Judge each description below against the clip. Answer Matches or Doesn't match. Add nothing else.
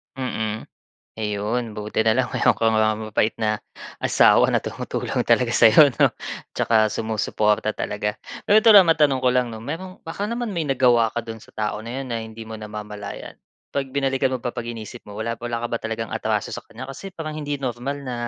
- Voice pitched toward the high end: Doesn't match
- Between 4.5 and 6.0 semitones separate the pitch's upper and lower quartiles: Doesn't match